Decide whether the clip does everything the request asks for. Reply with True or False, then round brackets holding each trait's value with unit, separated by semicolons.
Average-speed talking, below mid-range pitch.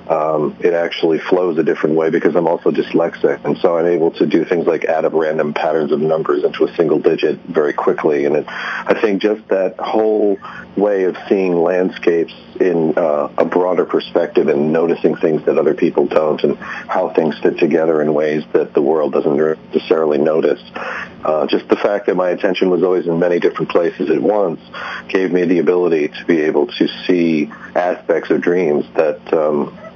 True (190 wpm; 105 Hz)